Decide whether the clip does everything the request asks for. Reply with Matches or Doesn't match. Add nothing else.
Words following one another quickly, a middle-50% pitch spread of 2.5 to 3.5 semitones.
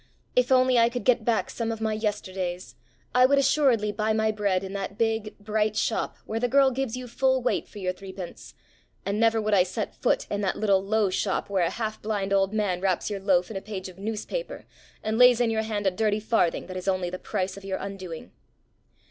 Matches